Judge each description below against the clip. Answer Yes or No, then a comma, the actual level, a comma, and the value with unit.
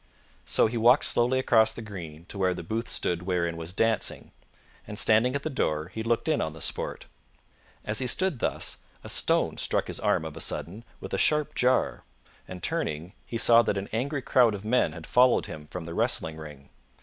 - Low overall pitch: Yes, low, 105 Hz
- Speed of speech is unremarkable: No, fast, 210 wpm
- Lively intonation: Yes, wide, 6.4 semitones